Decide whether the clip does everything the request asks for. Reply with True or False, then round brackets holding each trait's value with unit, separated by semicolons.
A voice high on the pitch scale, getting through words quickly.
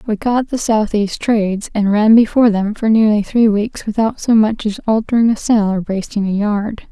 True (215 Hz; 210 wpm)